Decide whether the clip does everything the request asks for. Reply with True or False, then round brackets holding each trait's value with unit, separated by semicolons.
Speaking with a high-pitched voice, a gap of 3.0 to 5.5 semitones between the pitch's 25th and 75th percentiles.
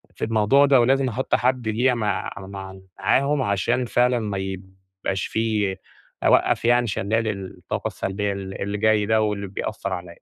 False (105 Hz; 3.7 semitones)